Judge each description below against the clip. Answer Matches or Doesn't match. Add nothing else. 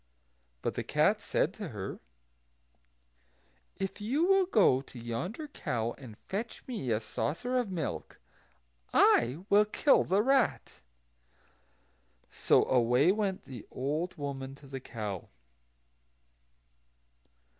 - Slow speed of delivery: Matches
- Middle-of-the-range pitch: Matches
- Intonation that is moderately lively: Doesn't match